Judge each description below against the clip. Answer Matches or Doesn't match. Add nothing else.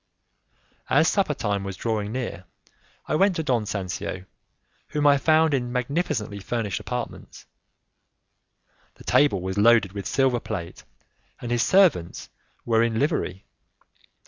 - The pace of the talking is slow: Matches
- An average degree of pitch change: Doesn't match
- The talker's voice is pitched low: Matches